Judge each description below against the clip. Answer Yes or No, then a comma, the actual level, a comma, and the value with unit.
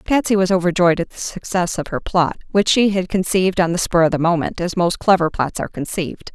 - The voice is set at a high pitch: No, medium, 180 Hz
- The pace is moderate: No, fast, 235 wpm